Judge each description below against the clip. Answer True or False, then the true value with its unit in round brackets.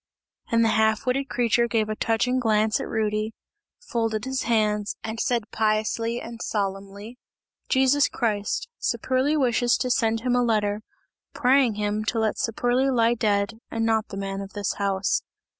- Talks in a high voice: True (225 Hz)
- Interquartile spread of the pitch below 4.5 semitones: True (2.4 semitones)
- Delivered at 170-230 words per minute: False (160 wpm)